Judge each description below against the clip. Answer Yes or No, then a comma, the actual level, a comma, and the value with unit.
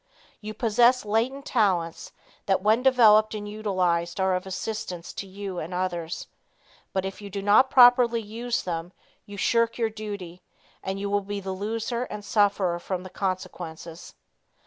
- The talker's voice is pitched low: No, high, 205 Hz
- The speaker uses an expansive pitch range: No, average, 3.1 semitones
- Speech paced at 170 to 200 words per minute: No, average, 160 wpm